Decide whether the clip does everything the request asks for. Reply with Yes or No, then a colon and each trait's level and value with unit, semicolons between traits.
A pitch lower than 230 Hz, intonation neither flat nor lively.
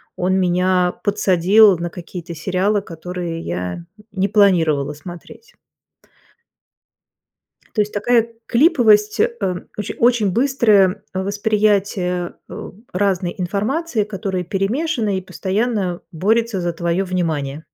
Yes: high, 190 Hz; average, 3.2 semitones